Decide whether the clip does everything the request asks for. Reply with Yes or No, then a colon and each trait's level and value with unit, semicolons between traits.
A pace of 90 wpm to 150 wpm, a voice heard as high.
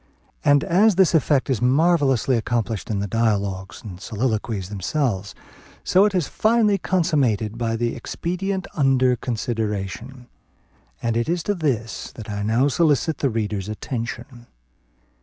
No: average, 140 wpm; low, 120 Hz